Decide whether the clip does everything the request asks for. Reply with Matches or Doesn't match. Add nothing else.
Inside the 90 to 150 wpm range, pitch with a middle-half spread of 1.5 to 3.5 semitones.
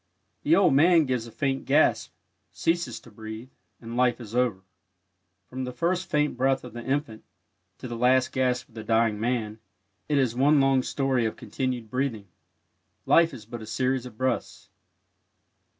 Doesn't match